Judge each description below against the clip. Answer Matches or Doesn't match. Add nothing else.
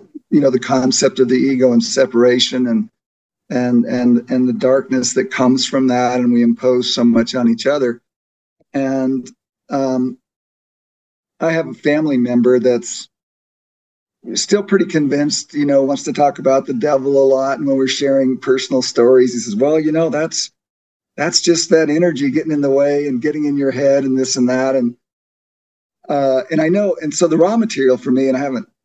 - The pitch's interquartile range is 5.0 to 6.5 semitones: Doesn't match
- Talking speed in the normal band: Matches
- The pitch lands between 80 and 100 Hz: Doesn't match